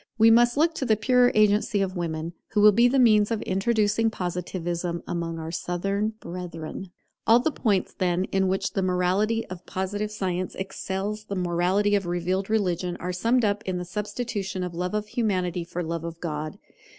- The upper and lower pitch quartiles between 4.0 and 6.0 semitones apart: No, average, 3.2 semitones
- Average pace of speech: Yes, average, 185 wpm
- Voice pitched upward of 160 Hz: Yes, high, 190 Hz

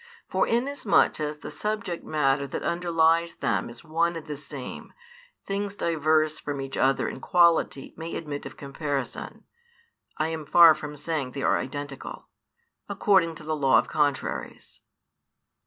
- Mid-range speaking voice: Yes, medium, 155 Hz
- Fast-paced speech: No, average, 150 wpm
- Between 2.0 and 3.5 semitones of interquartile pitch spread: Yes, average, 2.9 semitones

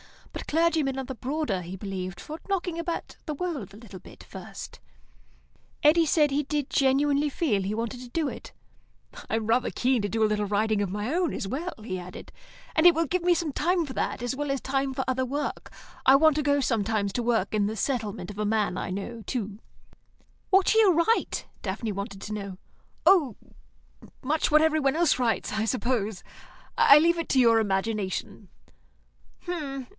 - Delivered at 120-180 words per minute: No, average, 190 wpm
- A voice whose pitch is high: Yes, very high, 255 Hz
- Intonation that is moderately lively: No, wide, 6.4 semitones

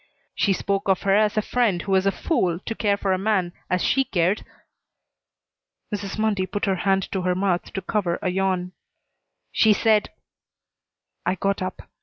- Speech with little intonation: Yes, narrow, 2.0 semitones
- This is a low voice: No, high, 195 Hz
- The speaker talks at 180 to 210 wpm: Yes, average, 185 wpm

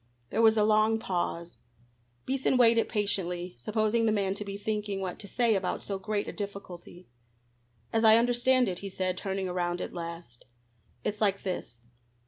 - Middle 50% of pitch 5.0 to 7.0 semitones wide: No, average, 3.2 semitones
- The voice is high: Yes, high, 200 Hz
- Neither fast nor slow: Yes, average, 170 wpm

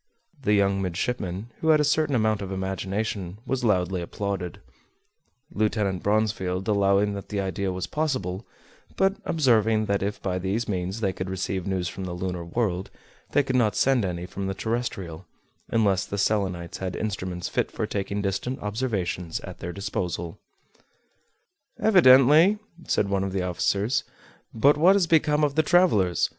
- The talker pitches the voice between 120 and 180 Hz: No, low, 100 Hz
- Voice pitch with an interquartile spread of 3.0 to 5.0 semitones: Yes, average, 4.3 semitones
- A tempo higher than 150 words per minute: Yes, average, 160 wpm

